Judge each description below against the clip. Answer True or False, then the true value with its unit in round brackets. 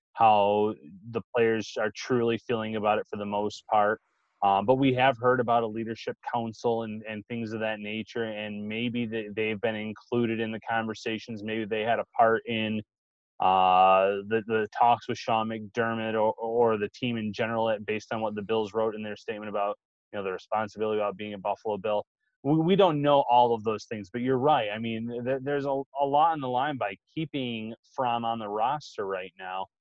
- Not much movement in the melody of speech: True (2.0 semitones)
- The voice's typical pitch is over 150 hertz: False (110 Hz)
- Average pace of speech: False (210 wpm)